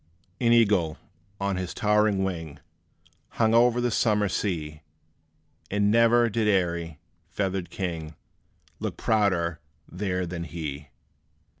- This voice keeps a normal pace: No, slow, 115 wpm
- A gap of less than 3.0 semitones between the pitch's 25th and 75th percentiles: No, average, 4.1 semitones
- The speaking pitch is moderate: No, very low, 95 Hz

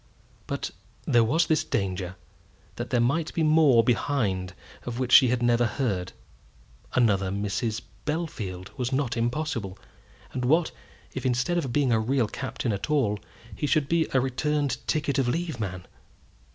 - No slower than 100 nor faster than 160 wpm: Yes, average, 155 wpm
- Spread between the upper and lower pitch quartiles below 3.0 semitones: No, average, 5.3 semitones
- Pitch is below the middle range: Yes, low, 125 Hz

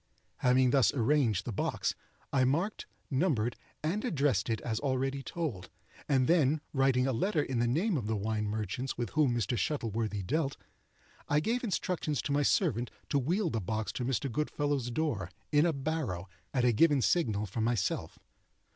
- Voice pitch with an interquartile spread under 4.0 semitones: No, average, 4.9 semitones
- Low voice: Yes, low, 130 Hz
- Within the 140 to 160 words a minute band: No, average, 175 wpm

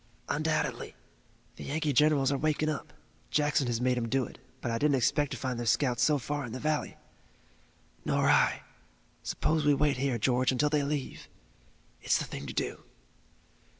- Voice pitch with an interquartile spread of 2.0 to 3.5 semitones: Yes, average, 3.0 semitones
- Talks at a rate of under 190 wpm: Yes, average, 180 wpm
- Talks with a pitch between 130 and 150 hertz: Yes, medium, 140 Hz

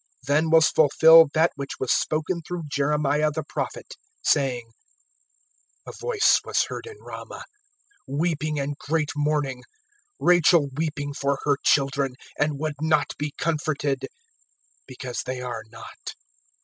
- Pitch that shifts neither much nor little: No, narrow, 2.3 semitones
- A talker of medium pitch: Yes, medium, 150 Hz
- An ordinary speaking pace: No, slow, 130 wpm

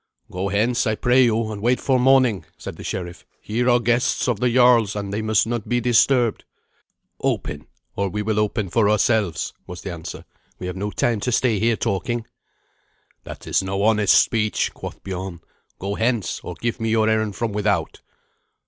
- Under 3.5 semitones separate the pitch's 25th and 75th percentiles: Yes, average, 3.0 semitones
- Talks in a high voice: No, low, 110 Hz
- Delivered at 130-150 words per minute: No, average, 185 wpm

